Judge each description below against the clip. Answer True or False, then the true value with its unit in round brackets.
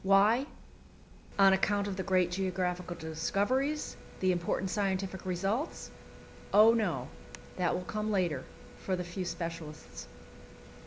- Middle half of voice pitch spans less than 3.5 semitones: True (2.4 semitones)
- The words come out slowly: True (120 wpm)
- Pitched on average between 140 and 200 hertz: True (190 Hz)